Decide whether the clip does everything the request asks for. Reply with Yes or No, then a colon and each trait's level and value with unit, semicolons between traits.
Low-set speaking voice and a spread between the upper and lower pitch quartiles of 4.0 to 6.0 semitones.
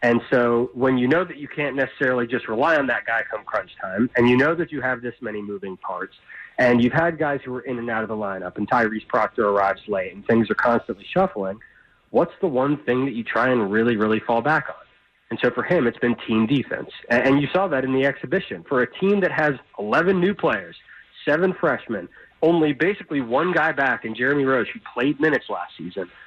Yes: low, 130 Hz; average, 4.7 semitones